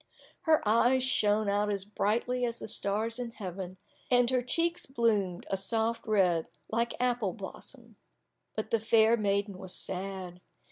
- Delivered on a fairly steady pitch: No, average, 3.2 semitones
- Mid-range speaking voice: No, high, 220 Hz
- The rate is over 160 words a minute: No, average, 150 wpm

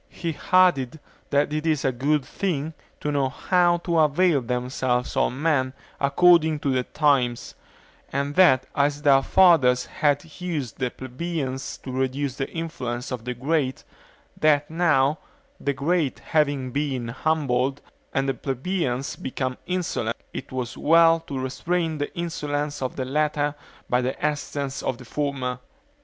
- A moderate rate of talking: Yes, average, 150 wpm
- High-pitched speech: No, medium, 140 Hz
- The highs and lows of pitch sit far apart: No, average, 3.4 semitones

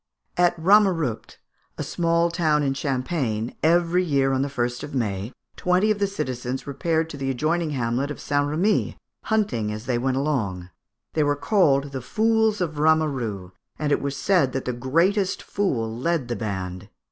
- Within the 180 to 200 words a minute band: No, average, 170 wpm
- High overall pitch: No, medium, 145 Hz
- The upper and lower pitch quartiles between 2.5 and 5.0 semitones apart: No, wide, 5.5 semitones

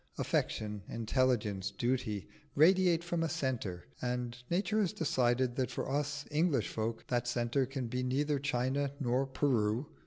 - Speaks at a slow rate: No, average, 145 wpm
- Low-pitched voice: Yes, low, 130 Hz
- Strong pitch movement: No, average, 3.5 semitones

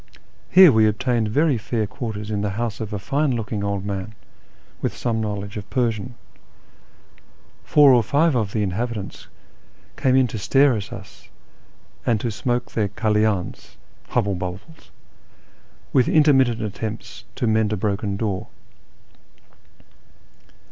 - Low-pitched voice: Yes, low, 110 Hz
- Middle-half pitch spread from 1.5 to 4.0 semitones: Yes, average, 3.2 semitones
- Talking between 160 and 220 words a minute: No, average, 140 wpm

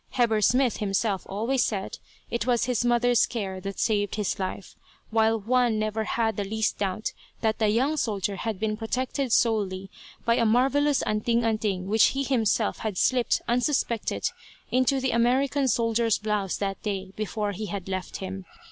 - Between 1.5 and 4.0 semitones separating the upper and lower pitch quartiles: Yes, average, 3.0 semitones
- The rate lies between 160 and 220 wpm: Yes, average, 165 wpm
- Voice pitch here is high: Yes, high, 220 Hz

